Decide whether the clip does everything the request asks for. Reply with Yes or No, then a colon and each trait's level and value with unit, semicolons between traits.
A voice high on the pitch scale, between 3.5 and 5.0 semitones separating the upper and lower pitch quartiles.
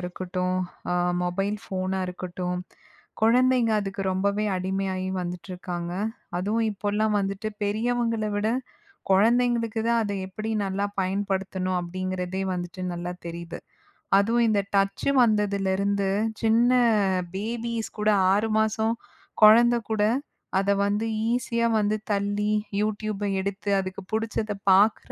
No: high, 200 Hz; average, 2.7 semitones